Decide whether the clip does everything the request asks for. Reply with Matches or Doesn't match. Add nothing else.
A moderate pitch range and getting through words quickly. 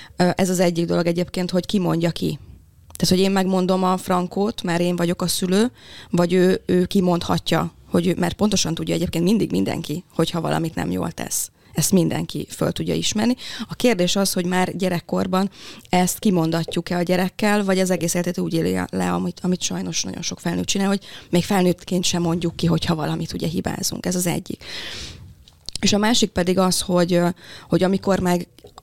Doesn't match